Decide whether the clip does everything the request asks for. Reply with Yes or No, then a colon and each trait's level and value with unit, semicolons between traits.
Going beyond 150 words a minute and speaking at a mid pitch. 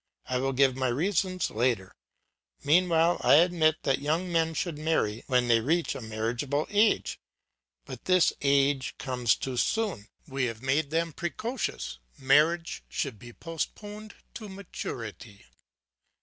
No: slow, 135 wpm; medium, 145 Hz